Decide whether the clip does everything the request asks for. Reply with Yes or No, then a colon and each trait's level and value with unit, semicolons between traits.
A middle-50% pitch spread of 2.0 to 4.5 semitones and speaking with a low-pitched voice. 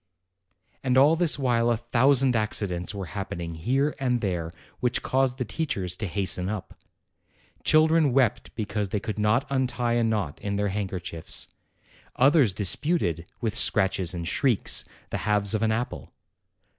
No: average, 5.3 semitones; low, 110 Hz